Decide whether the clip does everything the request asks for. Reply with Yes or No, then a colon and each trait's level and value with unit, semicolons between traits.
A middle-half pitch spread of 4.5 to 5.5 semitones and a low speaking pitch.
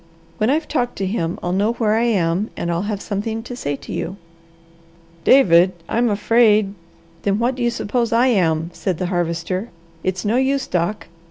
No: average, 4.9 semitones; high, 205 Hz